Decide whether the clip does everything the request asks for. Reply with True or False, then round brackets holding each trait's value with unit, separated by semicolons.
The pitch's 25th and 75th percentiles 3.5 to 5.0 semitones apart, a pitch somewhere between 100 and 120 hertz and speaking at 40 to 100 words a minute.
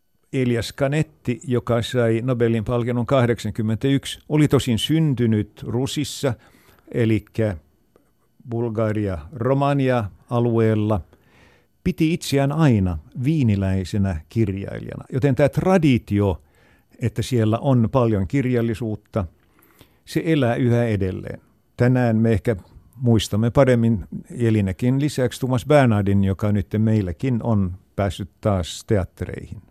True (3.9 semitones; 115 Hz; 95 wpm)